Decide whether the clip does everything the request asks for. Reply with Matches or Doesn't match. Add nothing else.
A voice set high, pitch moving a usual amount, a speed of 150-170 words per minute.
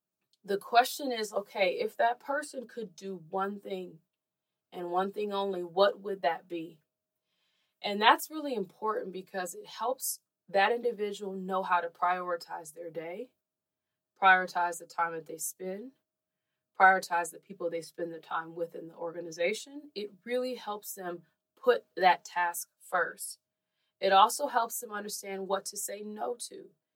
Matches